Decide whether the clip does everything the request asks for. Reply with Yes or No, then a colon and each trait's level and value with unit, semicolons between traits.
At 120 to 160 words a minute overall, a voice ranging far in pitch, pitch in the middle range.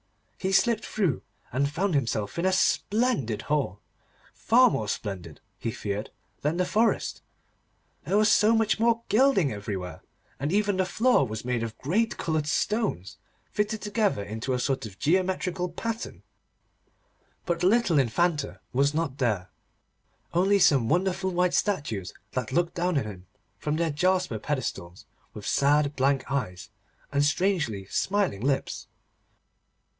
Yes: average, 145 wpm; wide, 8.7 semitones; medium, 150 Hz